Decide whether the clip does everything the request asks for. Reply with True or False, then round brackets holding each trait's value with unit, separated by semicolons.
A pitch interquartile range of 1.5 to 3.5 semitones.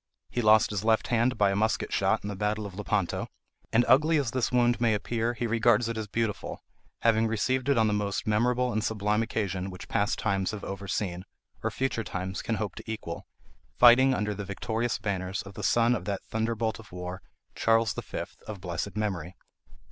True (2.6 semitones)